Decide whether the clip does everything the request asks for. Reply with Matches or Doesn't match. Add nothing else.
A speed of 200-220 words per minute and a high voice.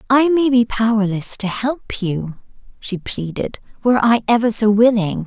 Doesn't match